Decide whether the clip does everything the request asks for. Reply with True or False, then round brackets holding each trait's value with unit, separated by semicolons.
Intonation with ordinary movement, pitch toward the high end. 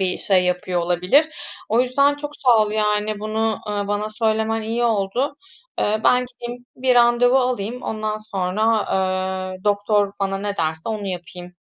True (3.6 semitones; 215 Hz)